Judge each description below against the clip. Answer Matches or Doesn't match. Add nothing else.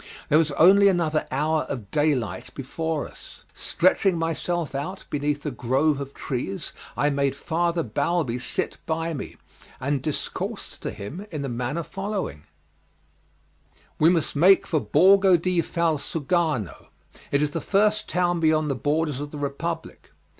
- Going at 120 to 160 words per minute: Matches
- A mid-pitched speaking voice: Matches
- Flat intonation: Doesn't match